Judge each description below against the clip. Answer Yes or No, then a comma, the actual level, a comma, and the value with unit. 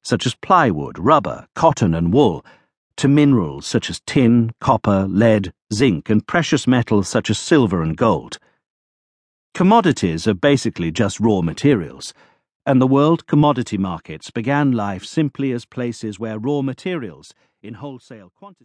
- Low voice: Yes, low, 120 Hz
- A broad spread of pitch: Yes, wide, 5.8 semitones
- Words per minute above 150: No, average, 145 wpm